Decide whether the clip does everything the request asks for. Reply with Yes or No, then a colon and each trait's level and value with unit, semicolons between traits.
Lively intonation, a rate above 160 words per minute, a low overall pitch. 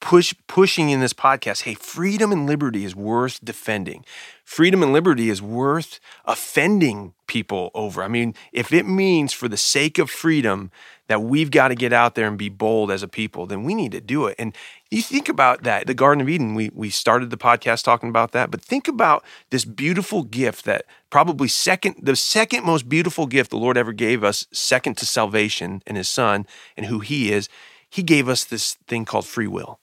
Yes: wide, 6.3 semitones; fast, 205 wpm; low, 125 Hz